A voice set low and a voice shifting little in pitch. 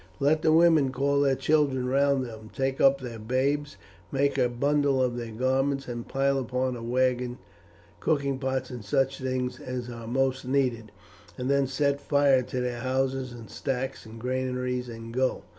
Yes: low, 130 Hz; narrow, 1.8 semitones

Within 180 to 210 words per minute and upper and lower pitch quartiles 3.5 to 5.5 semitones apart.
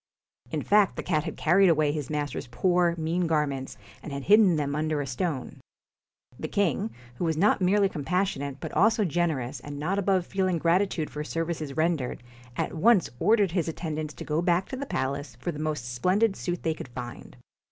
Yes: average, 190 wpm; average, 4.0 semitones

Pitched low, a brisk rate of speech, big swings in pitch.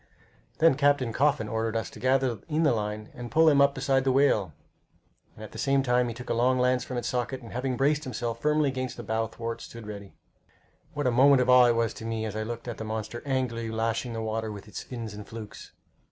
No: low, 120 Hz; fast, 240 wpm; average, 3.0 semitones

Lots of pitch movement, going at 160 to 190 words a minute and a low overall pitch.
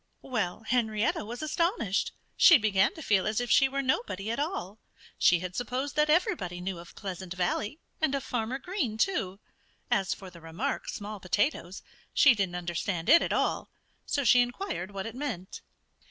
No: wide, 6.6 semitones; average, 175 wpm; high, 215 Hz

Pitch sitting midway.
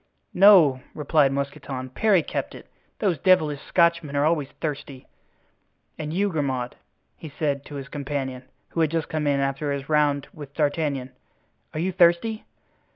Yes: medium, 150 Hz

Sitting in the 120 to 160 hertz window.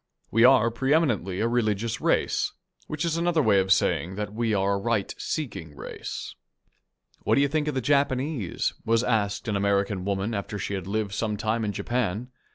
No: low, 110 Hz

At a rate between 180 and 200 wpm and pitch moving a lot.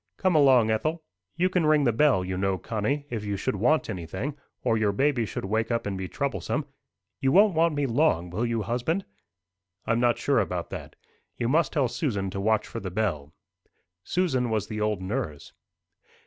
Yes: average, 190 wpm; wide, 6.3 semitones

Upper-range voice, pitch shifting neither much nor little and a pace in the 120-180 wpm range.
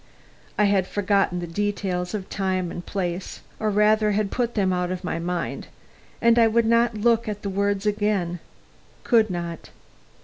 Yes: high, 200 Hz; average, 3.0 semitones; average, 170 wpm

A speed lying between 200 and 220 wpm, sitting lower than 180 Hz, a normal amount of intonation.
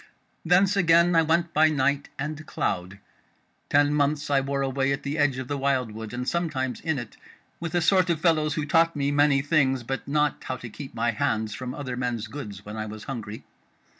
Yes: fast, 205 wpm; medium, 140 Hz; average, 3.7 semitones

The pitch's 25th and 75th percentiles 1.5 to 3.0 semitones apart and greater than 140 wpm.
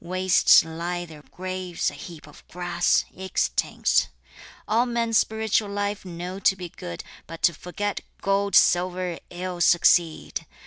No: narrow, 2.4 semitones; slow, 135 wpm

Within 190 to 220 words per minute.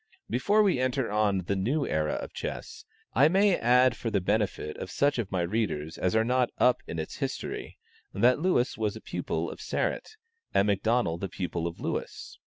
Yes: average, 195 wpm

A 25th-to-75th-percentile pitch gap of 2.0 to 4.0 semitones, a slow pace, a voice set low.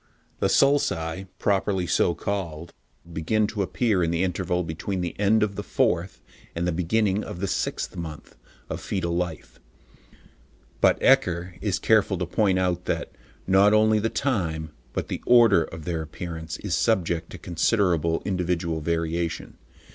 No: average, 3.4 semitones; average, 155 wpm; very low, 90 Hz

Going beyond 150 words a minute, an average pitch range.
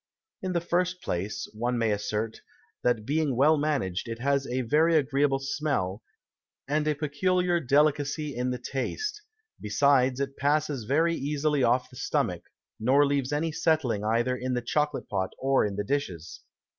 Yes: average, 160 wpm; average, 4.0 semitones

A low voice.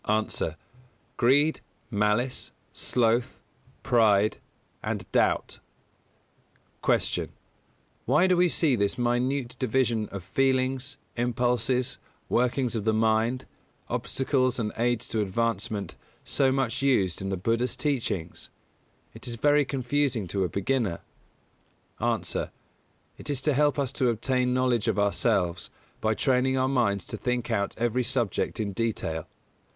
Yes: low, 120 Hz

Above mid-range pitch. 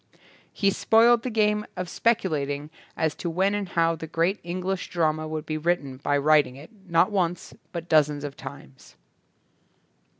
No: medium, 165 Hz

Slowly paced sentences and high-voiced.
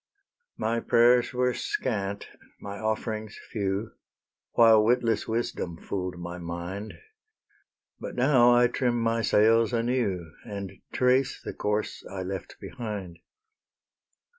No: slow, 115 wpm; low, 110 Hz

